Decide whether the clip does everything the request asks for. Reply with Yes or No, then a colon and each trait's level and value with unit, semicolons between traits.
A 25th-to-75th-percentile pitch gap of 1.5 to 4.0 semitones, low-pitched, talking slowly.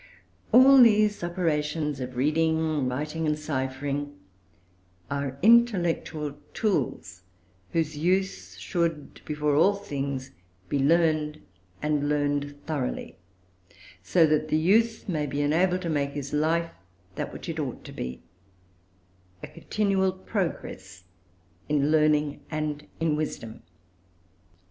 No: average, 2.9 semitones; medium, 150 Hz; slow, 115 wpm